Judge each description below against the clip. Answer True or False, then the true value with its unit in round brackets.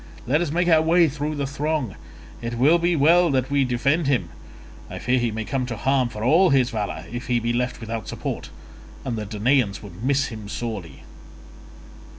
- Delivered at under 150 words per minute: False (195 wpm)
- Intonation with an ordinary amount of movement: True (4.3 semitones)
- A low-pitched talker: True (130 Hz)